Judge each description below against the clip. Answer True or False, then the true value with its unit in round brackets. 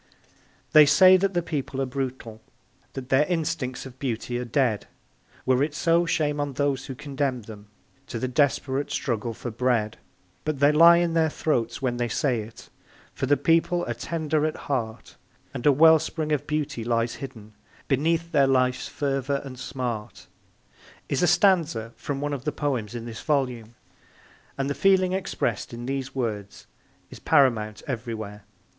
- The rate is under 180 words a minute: True (165 wpm)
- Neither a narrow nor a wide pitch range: True (4.0 semitones)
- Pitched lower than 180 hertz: True (135 Hz)